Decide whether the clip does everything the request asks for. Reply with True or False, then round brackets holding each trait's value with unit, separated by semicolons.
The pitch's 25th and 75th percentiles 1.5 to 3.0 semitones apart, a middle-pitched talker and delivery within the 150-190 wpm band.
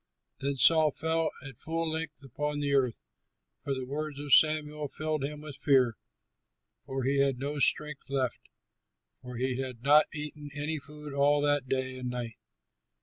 True (2.4 semitones; 145 Hz; 165 wpm)